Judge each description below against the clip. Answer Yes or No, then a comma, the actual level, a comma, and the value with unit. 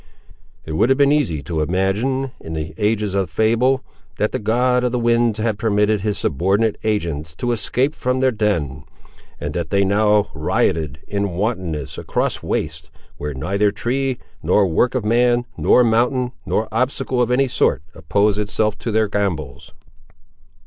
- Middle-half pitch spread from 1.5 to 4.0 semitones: No, average, 4.4 semitones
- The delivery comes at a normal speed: Yes, average, 165 wpm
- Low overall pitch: Yes, low, 105 Hz